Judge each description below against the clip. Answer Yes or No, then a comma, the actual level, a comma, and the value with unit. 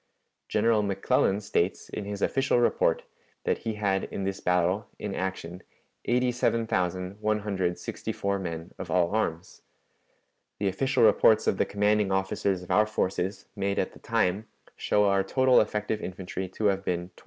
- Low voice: Yes, low, 100 Hz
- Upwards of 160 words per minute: No, average, 150 wpm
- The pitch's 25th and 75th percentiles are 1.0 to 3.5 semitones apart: Yes, narrow, 2.5 semitones